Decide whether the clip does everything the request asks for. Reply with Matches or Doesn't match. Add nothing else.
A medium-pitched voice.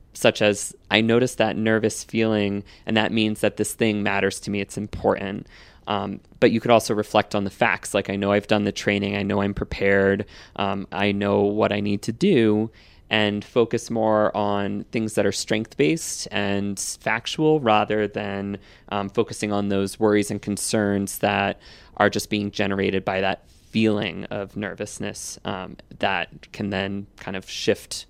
Doesn't match